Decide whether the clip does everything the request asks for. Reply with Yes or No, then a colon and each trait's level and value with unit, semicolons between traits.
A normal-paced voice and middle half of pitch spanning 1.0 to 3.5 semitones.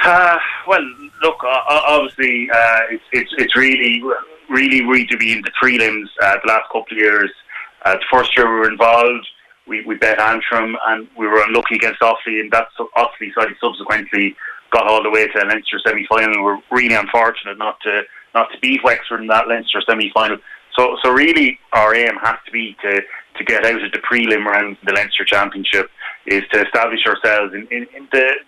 No: fast, 210 wpm; average, 2.7 semitones